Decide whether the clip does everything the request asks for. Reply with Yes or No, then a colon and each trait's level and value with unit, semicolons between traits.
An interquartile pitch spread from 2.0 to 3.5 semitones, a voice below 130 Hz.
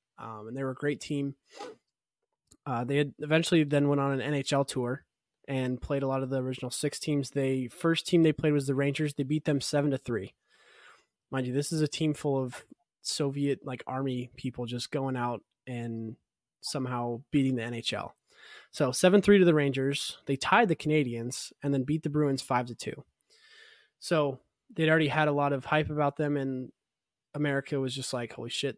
No: average, 2.8 semitones; medium, 140 Hz